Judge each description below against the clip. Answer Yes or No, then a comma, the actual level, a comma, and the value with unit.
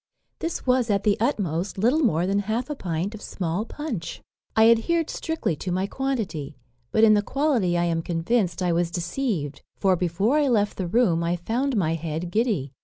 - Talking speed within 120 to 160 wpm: No, average, 190 wpm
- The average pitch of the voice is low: No, high, 200 Hz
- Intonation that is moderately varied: No, wide, 5.9 semitones